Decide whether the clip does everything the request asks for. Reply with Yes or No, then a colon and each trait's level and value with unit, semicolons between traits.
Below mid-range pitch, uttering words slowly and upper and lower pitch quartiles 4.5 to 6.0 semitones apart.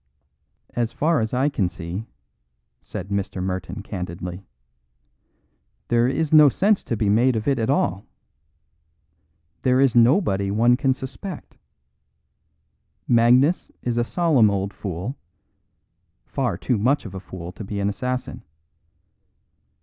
Yes: low, 115 Hz; slow, 130 wpm; average, 5.1 semitones